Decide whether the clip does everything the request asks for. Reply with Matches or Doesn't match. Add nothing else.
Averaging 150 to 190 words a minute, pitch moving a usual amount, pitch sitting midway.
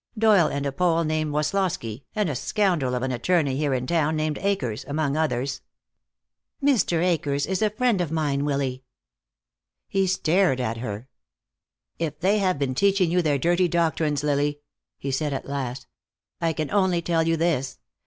Matches